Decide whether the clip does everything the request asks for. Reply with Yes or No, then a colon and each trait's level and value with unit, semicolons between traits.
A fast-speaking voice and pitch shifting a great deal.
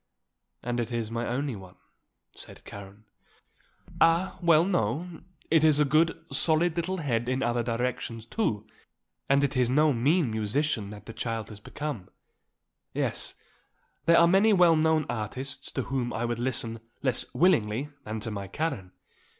No: average, 160 wpm; wide, 5.8 semitones